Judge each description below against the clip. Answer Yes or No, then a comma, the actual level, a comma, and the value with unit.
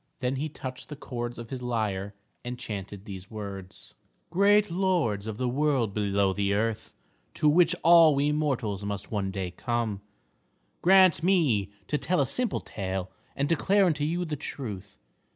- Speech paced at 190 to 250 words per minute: No, average, 165 wpm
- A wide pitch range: Yes, wide, 7.3 semitones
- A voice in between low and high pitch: No, low, 125 Hz